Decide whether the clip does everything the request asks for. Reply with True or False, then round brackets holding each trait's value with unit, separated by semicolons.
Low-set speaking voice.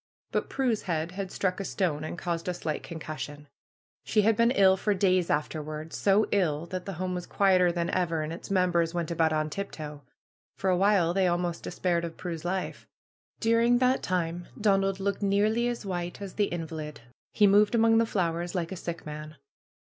False (180 Hz)